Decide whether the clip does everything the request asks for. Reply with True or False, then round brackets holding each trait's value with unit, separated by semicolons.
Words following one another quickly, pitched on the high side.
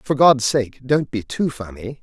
False (210 wpm; 125 Hz)